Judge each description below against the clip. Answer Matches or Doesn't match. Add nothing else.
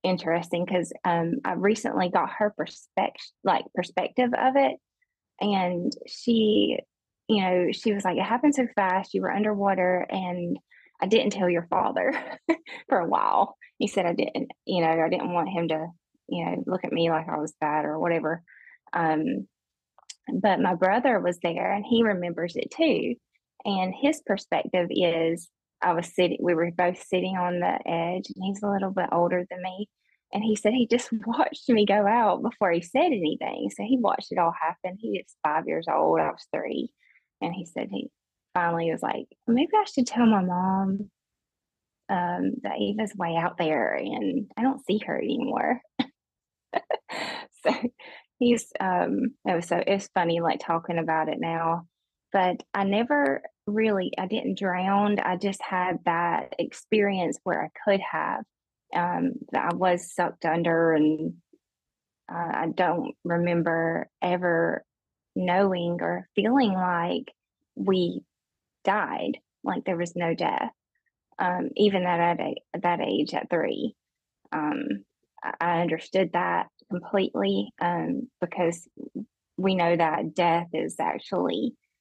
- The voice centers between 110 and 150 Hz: Doesn't match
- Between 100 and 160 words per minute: Matches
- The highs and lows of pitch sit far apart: Doesn't match